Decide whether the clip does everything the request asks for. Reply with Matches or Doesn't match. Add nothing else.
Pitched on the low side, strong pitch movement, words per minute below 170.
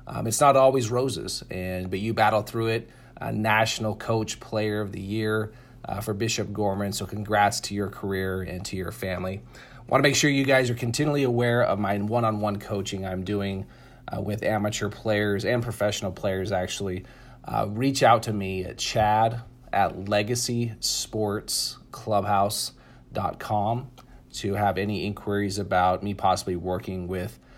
Doesn't match